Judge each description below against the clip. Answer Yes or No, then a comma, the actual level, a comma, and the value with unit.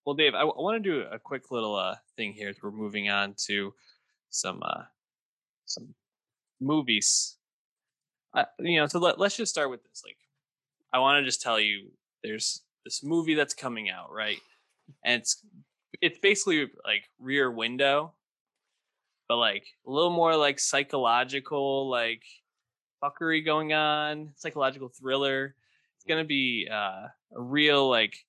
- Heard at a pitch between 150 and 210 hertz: No, medium, 140 Hz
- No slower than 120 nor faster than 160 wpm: Yes, average, 155 wpm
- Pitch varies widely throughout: No, average, 4.0 semitones